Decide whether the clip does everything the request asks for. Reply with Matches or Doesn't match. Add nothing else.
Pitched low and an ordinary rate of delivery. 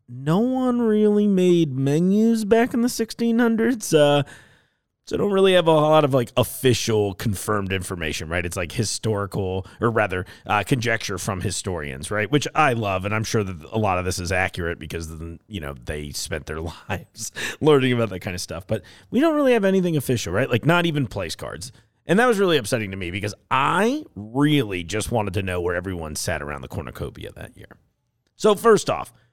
Matches